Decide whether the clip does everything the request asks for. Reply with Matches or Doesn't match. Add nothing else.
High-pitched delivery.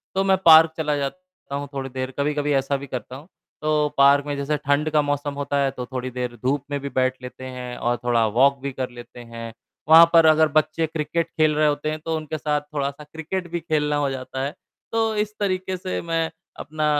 Doesn't match